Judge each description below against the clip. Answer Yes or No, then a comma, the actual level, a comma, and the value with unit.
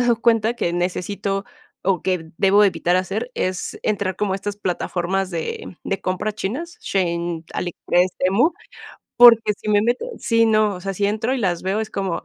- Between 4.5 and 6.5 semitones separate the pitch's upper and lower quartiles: No, average, 3.0 semitones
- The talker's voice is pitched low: No, high, 195 Hz